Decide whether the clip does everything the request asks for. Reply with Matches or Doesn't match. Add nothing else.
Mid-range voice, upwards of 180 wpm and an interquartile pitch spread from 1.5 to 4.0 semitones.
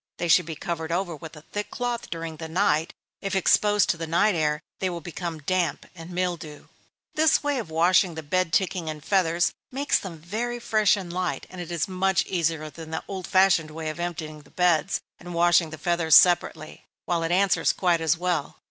Matches